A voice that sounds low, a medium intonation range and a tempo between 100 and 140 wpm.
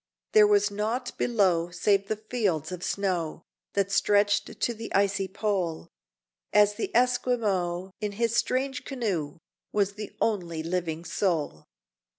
No: high, 200 Hz; average, 3.6 semitones; slow, 135 wpm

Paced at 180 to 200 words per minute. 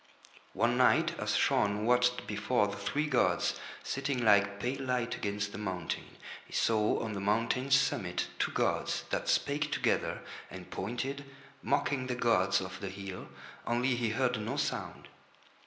No: average, 155 wpm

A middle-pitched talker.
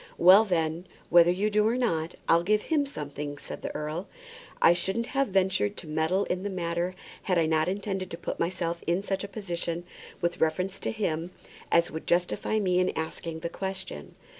Yes: medium, 180 Hz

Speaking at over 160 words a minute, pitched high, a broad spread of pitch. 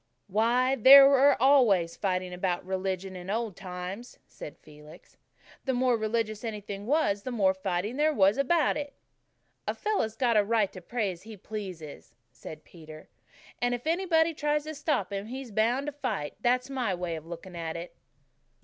Yes: average, 175 wpm; high, 215 Hz; wide, 6.0 semitones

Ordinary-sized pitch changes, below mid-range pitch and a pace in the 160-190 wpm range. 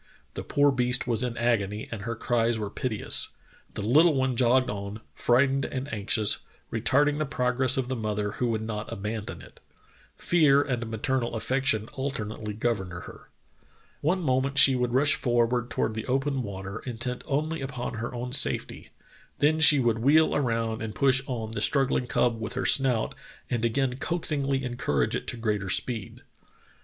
Yes: average, 3.3 semitones; low, 125 Hz; average, 170 wpm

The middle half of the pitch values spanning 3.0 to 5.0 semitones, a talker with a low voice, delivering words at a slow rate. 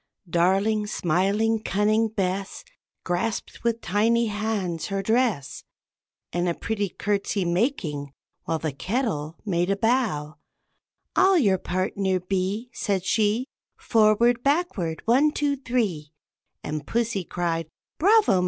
No: average, 4.6 semitones; high, 200 Hz; slow, 115 wpm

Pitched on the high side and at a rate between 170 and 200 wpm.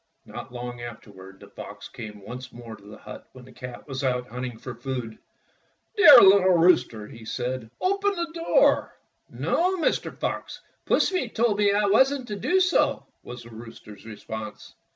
No: low, 125 Hz; average, 175 wpm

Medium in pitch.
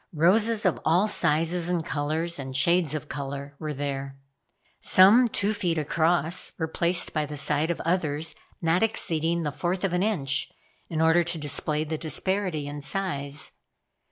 Yes: medium, 160 Hz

